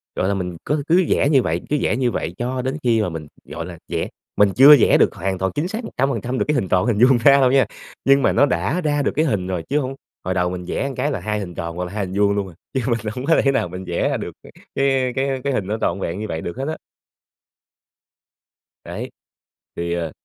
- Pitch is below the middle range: Yes, low, 115 Hz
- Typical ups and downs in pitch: No, wide, 6.9 semitones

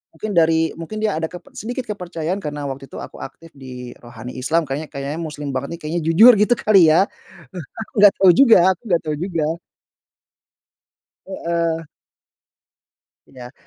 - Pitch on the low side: No, medium, 165 Hz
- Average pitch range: Yes, average, 4.2 semitones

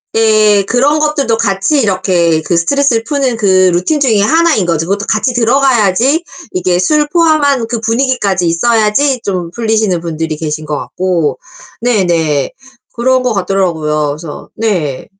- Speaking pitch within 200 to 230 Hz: Yes, high, 210 Hz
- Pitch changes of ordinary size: No, wide, 6.3 semitones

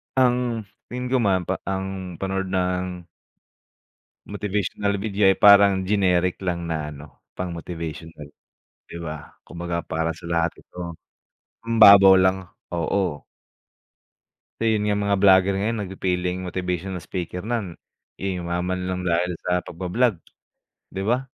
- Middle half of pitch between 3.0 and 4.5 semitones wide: No, narrow, 2.5 semitones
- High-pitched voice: No, very low, 95 Hz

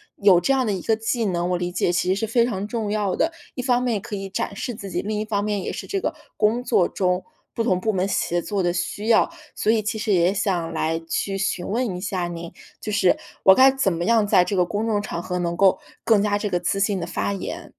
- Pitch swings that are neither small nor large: Yes, average, 3.5 semitones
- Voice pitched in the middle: No, high, 200 Hz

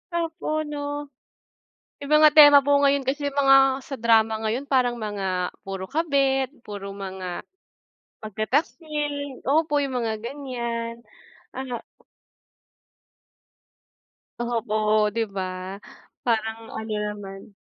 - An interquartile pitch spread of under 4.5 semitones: No, average, 4.9 semitones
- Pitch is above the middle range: Yes, high, 240 Hz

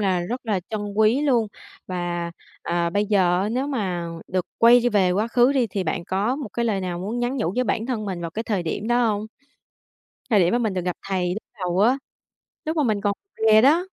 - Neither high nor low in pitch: No, high, 210 Hz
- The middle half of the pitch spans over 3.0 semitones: Yes, average, 4.8 semitones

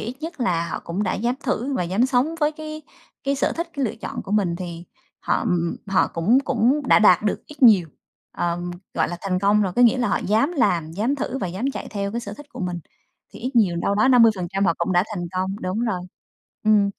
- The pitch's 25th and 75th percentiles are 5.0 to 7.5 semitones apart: Yes, wide, 5.5 semitones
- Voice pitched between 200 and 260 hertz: Yes, high, 210 Hz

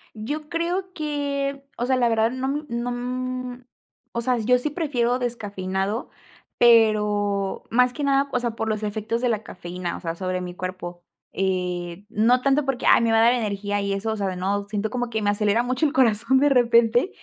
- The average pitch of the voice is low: No, high, 230 Hz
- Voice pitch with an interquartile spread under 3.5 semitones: No, average, 3.8 semitones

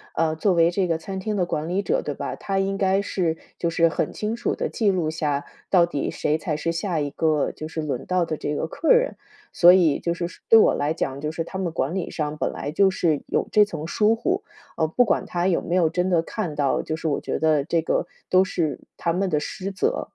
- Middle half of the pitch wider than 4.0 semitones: No, average, 3.5 semitones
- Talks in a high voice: No, medium, 170 Hz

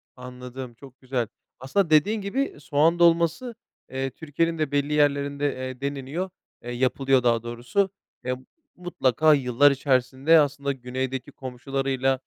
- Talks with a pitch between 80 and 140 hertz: Yes, low, 135 Hz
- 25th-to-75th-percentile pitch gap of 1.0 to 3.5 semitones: Yes, average, 3.2 semitones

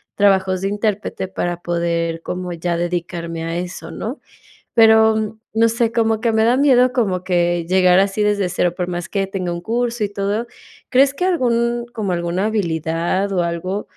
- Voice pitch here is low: No, high, 195 Hz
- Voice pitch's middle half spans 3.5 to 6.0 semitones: Yes, average, 4.2 semitones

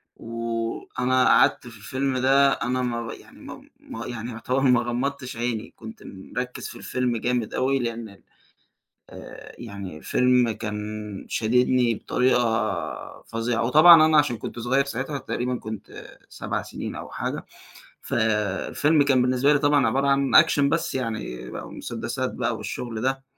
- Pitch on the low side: Yes, low, 125 Hz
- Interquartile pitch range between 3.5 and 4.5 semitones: No, average, 2.7 semitones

